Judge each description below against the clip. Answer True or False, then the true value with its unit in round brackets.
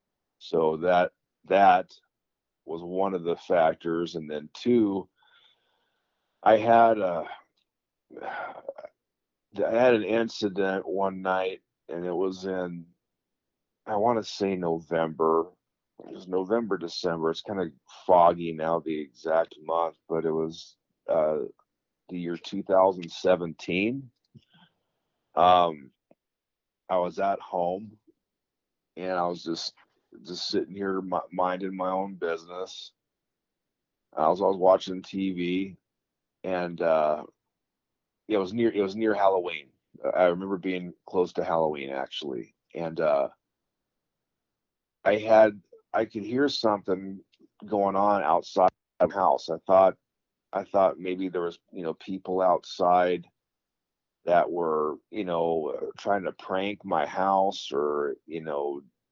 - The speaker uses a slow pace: True (125 wpm)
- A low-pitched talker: True (90 Hz)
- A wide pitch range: False (2.6 semitones)